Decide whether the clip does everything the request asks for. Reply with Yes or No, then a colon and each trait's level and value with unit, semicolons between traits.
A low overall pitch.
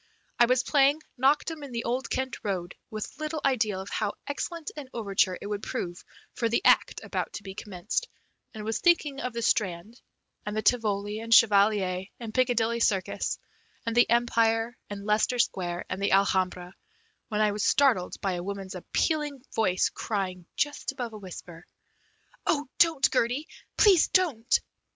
No: high, 225 Hz